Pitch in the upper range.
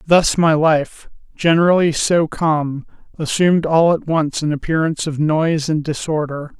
No: medium, 155 Hz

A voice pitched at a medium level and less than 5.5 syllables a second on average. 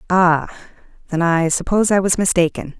No: medium, 175 Hz; 5.6 syllables/s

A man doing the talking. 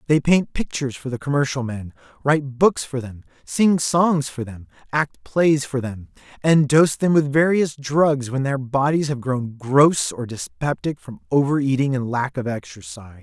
Yes: male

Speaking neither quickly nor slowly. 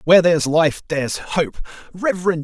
Yes: average, 150 wpm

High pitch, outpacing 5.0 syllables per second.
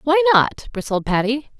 No: very high, 270 Hz; 4.6 syllables/s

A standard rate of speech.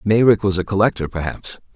Yes: average, 170 wpm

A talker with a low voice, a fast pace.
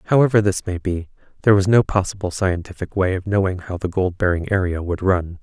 Yes: very low, 95 Hz; fast, 210 wpm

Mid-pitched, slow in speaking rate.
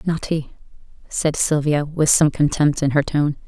No: medium, 150 Hz; average, 175 wpm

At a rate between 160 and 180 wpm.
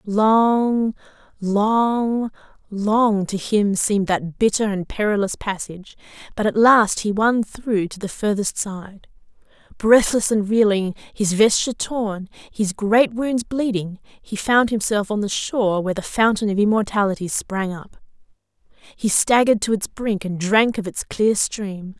No: average, 150 wpm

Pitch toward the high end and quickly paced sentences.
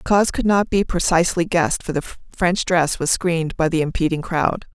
No: medium, 170 Hz; fast, 215 wpm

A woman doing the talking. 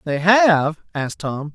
No: male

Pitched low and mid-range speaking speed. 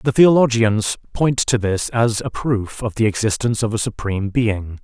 Yes: low, 110 Hz; average, 185 wpm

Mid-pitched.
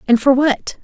No: very high, 260 Hz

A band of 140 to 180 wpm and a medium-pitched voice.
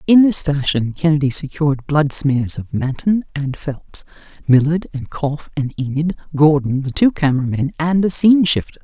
Yes: average, 170 wpm; medium, 150 Hz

